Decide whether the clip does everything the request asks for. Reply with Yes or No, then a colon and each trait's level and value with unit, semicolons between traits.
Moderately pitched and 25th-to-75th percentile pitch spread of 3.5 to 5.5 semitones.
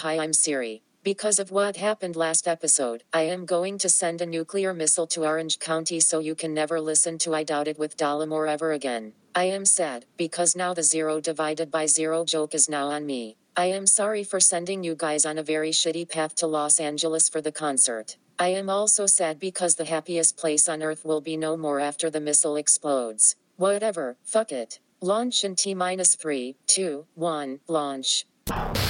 No: medium, 160 Hz; narrow, 2.6 semitones